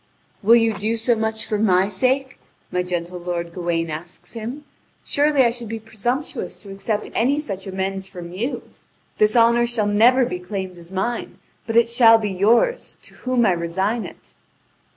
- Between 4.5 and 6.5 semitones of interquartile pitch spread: No, average, 4.1 semitones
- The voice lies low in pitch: No, high, 215 Hz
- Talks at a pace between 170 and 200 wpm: Yes, average, 175 wpm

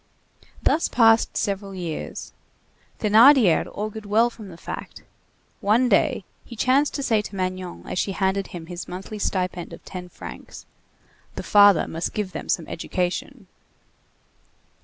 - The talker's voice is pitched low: No, high, 200 Hz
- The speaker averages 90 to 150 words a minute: Yes, average, 140 wpm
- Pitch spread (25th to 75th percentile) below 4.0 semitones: Yes, average, 3.4 semitones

